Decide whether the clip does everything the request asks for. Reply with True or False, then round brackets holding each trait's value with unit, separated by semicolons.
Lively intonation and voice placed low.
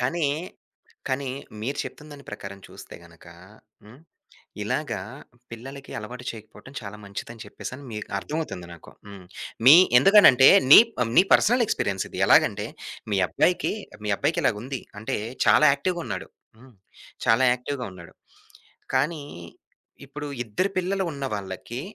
True (5.7 semitones; 130 Hz)